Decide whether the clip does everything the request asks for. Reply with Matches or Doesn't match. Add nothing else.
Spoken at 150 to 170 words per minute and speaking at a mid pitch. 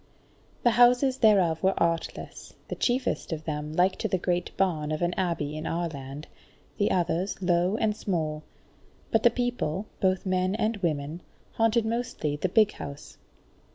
Matches